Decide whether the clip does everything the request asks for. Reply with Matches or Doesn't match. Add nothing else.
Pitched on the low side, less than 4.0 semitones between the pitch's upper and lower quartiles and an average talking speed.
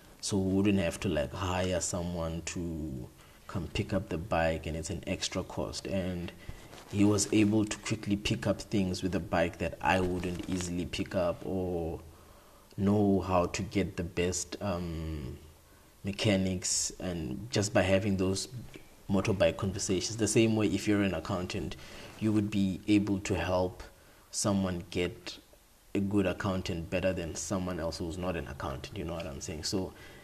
Matches